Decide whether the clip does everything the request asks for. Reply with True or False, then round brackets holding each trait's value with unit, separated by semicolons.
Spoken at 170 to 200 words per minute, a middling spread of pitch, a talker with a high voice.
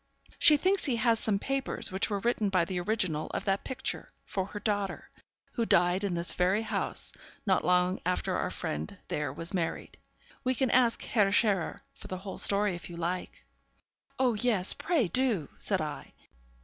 True (180 wpm; 4.4 semitones; 200 Hz)